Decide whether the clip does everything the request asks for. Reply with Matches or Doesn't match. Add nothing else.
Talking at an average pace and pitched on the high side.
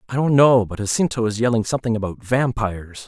Doesn't match